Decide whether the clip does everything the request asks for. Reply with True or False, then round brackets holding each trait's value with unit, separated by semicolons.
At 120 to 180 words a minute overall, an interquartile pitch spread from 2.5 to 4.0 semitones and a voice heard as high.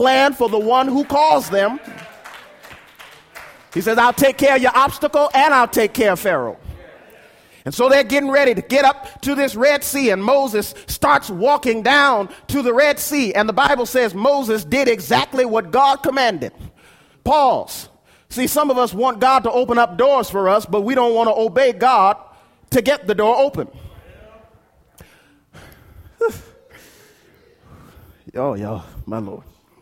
True (165 wpm; 3.3 semitones; 255 Hz)